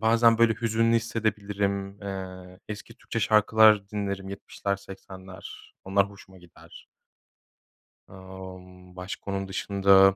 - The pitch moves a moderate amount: No, narrow, 2.0 semitones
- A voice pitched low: Yes, low, 100 Hz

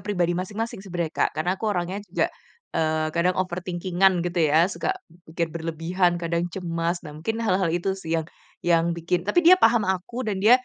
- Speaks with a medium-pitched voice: Yes, medium, 175 Hz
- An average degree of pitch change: No, narrow, 2.3 semitones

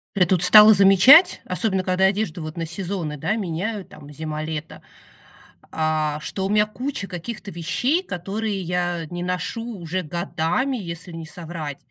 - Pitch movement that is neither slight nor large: Yes, average, 3.9 semitones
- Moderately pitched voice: Yes, medium, 180 Hz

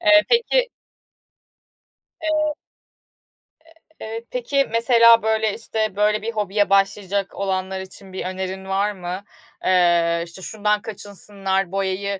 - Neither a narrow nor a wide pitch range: Yes, average, 3.0 semitones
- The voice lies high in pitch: Yes, high, 200 Hz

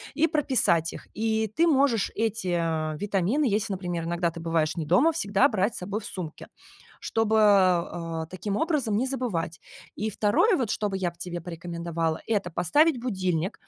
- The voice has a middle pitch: No, high, 195 Hz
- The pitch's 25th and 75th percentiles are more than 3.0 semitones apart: Yes, average, 4.8 semitones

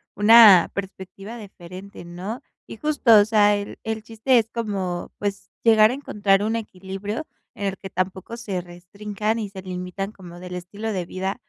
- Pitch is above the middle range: Yes, high, 200 Hz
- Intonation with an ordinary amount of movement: Yes, average, 3.0 semitones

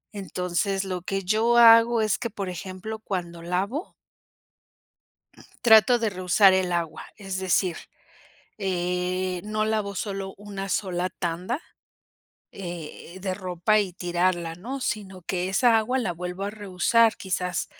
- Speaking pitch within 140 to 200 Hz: Yes, high, 190 Hz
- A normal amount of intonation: Yes, average, 3.0 semitones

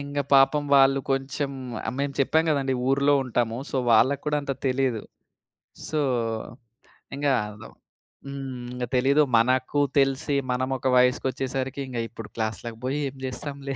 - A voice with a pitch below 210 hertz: Yes, low, 135 Hz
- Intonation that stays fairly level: Yes, narrow, 1.8 semitones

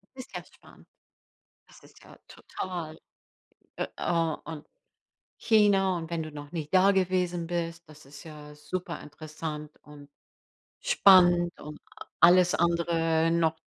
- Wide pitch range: No, average, 2.7 semitones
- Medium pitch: Yes, medium, 165 Hz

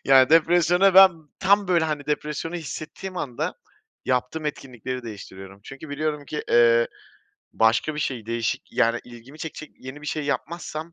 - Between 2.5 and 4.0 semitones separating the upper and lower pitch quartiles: No, average, 4.8 semitones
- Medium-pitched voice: Yes, medium, 150 Hz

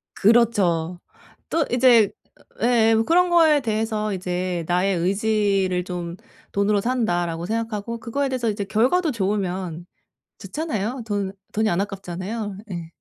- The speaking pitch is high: Yes, high, 205 Hz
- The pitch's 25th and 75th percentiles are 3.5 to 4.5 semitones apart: Yes, average, 4.1 semitones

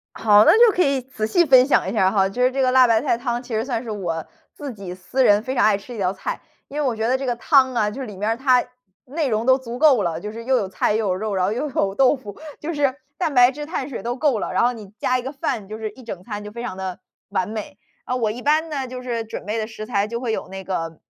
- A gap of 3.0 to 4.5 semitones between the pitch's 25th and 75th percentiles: Yes, average, 4.0 semitones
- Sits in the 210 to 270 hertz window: Yes, high, 235 Hz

